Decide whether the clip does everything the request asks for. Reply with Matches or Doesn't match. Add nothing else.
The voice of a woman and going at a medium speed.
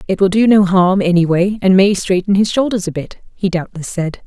Doesn't match